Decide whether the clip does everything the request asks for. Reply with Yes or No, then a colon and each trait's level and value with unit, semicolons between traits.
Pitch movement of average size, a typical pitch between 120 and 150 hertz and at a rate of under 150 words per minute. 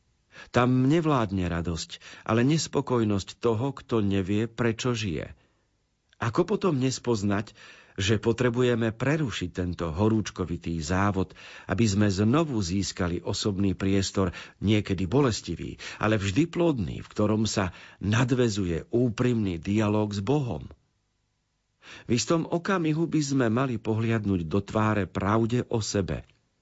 No: average, 4.1 semitones; low, 110 Hz; average, 115 wpm